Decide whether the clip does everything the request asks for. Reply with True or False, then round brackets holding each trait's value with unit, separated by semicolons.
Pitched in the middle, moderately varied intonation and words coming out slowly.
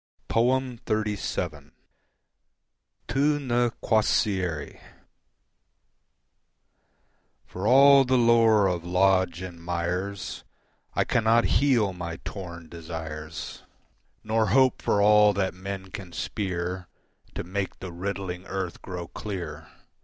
False (95 Hz; 4.2 semitones; 100 wpm)